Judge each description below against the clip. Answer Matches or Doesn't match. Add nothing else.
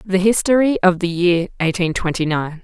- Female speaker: Matches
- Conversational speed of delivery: Matches